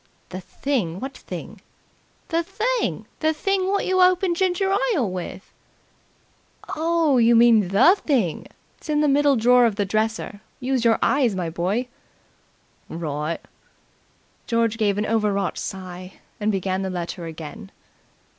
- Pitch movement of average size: No, wide, 7.8 semitones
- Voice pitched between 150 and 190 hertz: No, high, 225 Hz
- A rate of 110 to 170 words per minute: Yes, average, 140 wpm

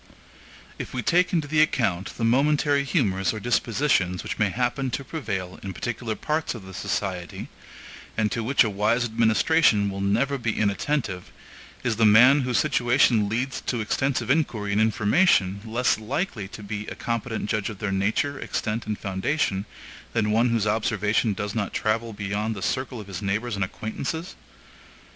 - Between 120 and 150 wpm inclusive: No, average, 170 wpm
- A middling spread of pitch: Yes, average, 3.9 semitones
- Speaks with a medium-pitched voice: No, low, 110 Hz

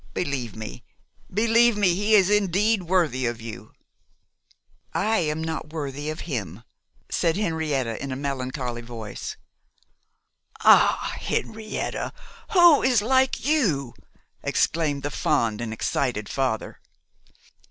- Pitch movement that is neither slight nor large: No, wide, 8.7 semitones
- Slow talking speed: Yes, slow, 115 wpm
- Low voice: No, medium, 155 Hz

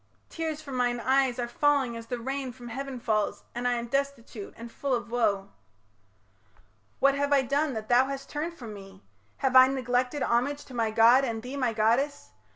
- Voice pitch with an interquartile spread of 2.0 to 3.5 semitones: Yes, average, 2.9 semitones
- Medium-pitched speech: No, very high, 250 Hz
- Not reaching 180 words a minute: No, average, 195 wpm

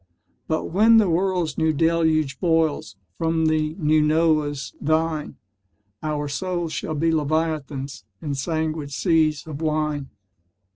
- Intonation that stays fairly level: Yes, narrow, 1.6 semitones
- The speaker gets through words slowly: Yes, slow, 125 wpm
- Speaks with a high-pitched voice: No, medium, 155 Hz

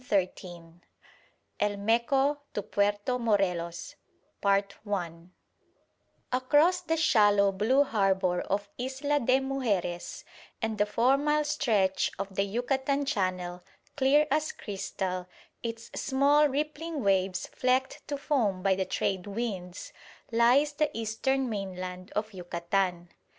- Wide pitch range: Yes, wide, 5.9 semitones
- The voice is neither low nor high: No, high, 210 Hz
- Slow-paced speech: Yes, slow, 115 wpm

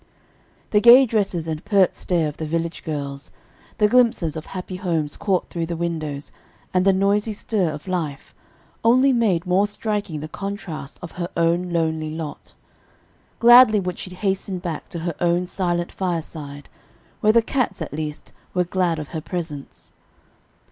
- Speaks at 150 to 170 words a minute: Yes, average, 160 wpm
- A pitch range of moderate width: Yes, average, 4.0 semitones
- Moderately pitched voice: Yes, medium, 175 Hz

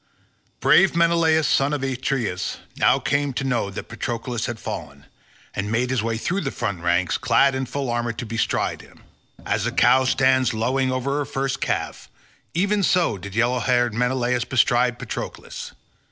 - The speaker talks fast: No, average, 170 wpm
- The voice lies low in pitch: Yes, low, 125 Hz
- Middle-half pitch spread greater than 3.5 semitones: No, average, 2.8 semitones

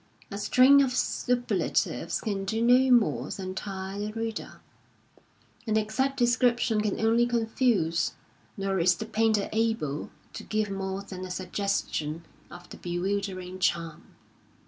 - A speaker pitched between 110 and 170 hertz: No, high, 205 Hz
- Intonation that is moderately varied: Yes, average, 3.5 semitones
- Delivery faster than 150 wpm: No, slow, 135 wpm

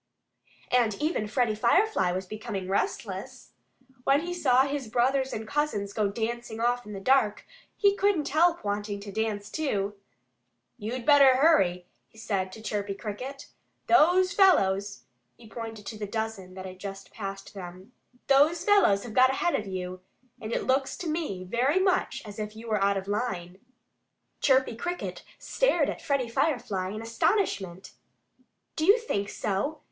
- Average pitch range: No, wide, 5.9 semitones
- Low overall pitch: No, high, 225 Hz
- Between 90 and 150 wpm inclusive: No, average, 160 wpm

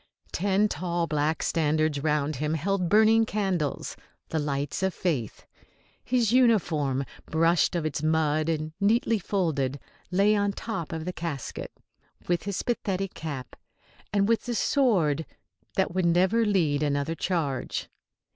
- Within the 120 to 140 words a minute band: Yes, slow, 135 wpm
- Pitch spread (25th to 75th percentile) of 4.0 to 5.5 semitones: Yes, average, 4.9 semitones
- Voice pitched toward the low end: No, medium, 170 Hz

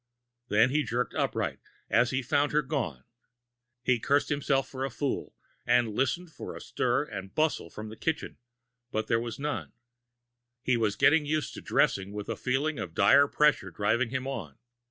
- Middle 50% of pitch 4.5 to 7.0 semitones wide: Yes, average, 4.8 semitones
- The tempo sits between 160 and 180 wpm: Yes, average, 175 wpm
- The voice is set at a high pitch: No, low, 130 Hz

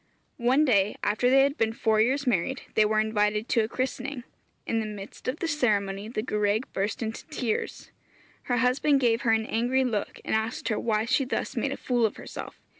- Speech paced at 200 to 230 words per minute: Yes, fast, 205 wpm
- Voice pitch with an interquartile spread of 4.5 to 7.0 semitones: No, average, 3.1 semitones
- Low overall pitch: No, high, 225 Hz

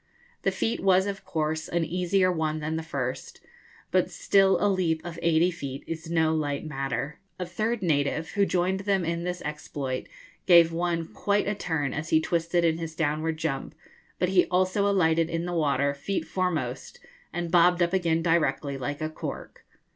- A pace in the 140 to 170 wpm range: No, average, 180 wpm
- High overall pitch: No, medium, 165 Hz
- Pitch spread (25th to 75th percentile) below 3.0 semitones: Yes, narrow, 2.5 semitones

